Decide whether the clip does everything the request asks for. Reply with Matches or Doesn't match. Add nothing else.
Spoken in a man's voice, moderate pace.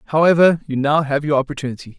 Matches